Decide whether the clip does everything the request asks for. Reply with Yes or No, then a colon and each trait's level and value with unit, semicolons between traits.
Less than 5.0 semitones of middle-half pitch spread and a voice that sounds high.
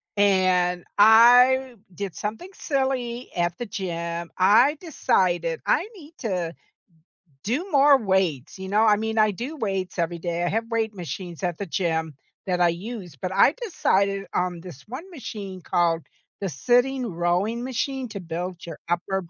No: wide, 5.6 semitones; high, 195 Hz